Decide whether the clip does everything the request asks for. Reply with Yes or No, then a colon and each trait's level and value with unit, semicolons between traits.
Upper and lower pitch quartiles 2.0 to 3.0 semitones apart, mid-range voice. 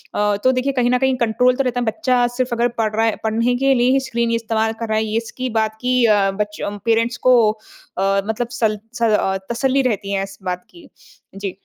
No: average, 2.7 semitones; high, 230 Hz